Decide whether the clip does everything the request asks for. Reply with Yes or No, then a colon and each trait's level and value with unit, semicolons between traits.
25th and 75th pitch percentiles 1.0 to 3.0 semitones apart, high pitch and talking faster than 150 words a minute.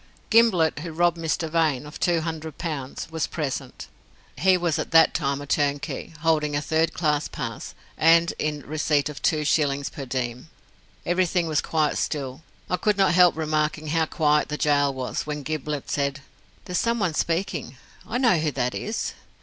No: narrow, 2.4 semitones; medium, 155 Hz; average, 175 wpm